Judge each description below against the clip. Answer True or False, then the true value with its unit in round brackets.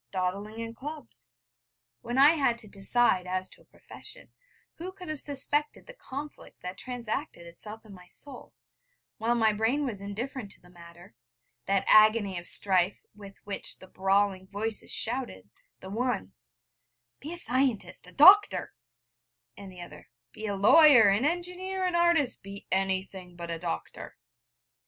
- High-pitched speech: True (215 Hz)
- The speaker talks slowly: False (155 wpm)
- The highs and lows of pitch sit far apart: True (6.4 semitones)